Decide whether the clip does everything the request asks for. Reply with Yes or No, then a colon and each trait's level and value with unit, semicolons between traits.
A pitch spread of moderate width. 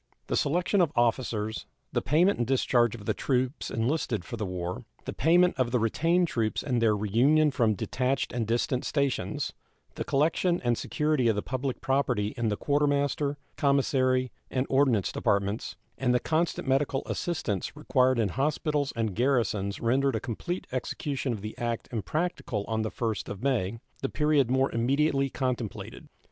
Yes: average, 3.9 semitones